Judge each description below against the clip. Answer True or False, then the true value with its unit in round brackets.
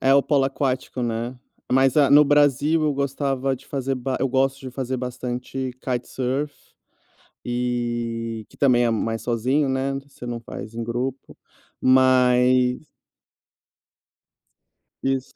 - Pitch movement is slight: True (1.8 semitones)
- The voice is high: False (130 Hz)